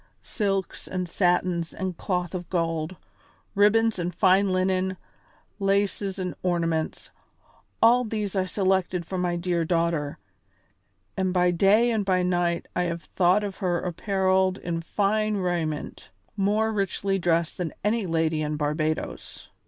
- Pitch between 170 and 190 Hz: Yes, medium, 185 Hz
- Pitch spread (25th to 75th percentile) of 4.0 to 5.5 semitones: No, narrow, 2.5 semitones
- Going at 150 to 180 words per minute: No, slow, 135 wpm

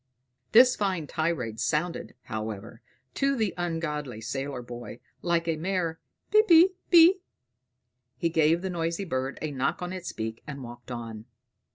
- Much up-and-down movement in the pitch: Yes, wide, 6.8 semitones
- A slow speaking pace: No, average, 145 wpm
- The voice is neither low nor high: Yes, medium, 160 Hz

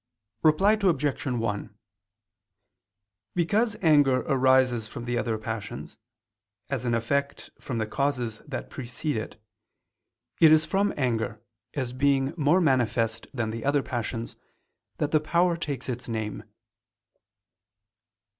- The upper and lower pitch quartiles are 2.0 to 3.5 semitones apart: No, average, 4.7 semitones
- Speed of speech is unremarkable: No, slow, 120 wpm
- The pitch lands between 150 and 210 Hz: No, low, 130 Hz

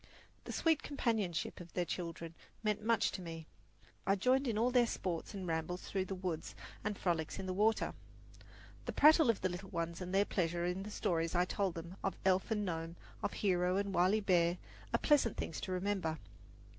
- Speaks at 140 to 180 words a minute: No, average, 195 wpm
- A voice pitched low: No, medium, 185 Hz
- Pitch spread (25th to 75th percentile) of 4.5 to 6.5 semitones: No, average, 3.4 semitones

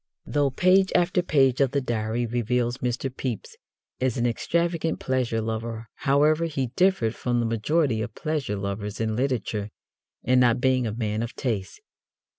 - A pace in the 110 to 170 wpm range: Yes, average, 160 wpm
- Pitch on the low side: Yes, low, 125 Hz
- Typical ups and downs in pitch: Yes, average, 3.8 semitones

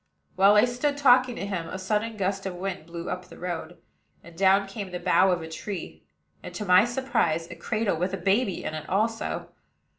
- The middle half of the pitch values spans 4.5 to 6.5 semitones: No, average, 3.4 semitones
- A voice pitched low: No, high, 195 Hz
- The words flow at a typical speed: No, fast, 210 wpm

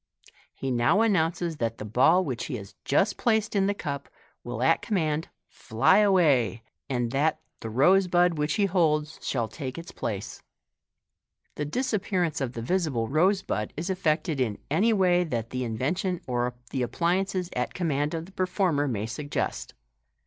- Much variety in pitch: Yes, wide, 6.9 semitones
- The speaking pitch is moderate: Yes, medium, 155 Hz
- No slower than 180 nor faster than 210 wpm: No, average, 170 wpm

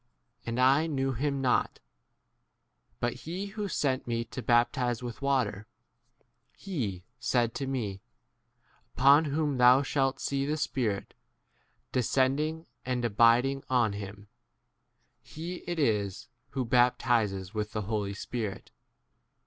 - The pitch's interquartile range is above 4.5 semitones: No, average, 3.6 semitones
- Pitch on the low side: Yes, low, 125 Hz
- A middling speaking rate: No, slow, 125 wpm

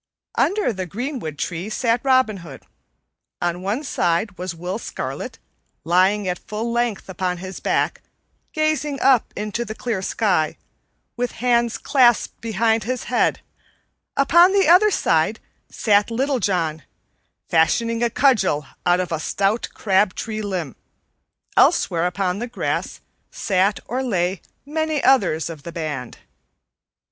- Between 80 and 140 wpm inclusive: Yes, slow, 135 wpm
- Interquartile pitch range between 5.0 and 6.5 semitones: Yes, wide, 5.4 semitones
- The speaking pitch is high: Yes, high, 210 Hz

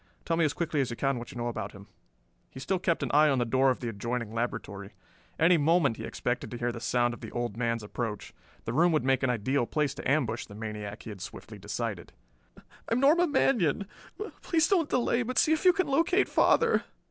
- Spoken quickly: Yes, fast, 230 wpm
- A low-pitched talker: Yes, low, 130 Hz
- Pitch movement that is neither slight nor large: No, wide, 7.2 semitones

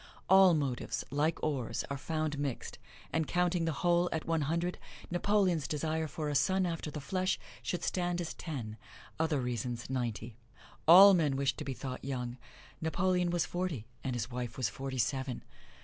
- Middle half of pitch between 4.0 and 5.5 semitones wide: Yes, average, 5.0 semitones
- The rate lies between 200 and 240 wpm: No, average, 170 wpm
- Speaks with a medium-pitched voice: Yes, medium, 150 Hz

